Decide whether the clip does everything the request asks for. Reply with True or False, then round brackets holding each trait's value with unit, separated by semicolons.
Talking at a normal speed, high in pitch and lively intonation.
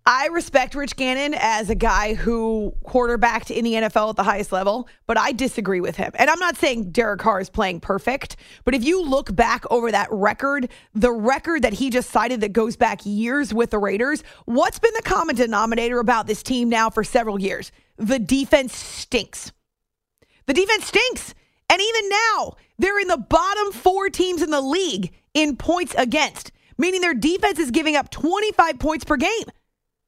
True (190 wpm; 255 Hz; 6.5 semitones)